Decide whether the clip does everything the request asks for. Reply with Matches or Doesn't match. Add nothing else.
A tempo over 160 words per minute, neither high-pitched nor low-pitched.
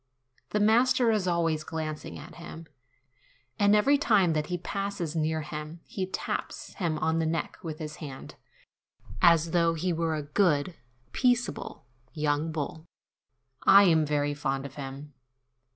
Doesn't match